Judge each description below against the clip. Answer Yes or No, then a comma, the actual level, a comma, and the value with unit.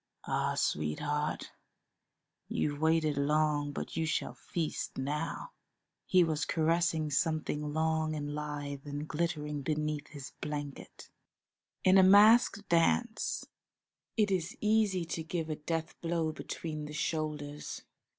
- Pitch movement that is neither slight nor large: No, narrow, 2.2 semitones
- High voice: No, medium, 155 Hz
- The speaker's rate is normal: No, slow, 120 wpm